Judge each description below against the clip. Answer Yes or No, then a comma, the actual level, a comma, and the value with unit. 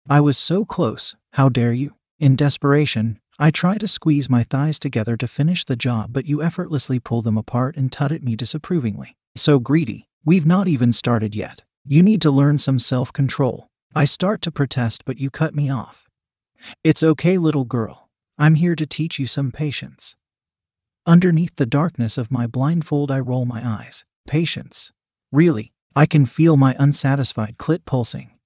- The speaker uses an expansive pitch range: No, average, 4.1 semitones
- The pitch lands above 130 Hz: Yes, medium, 140 Hz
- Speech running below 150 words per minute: No, average, 175 wpm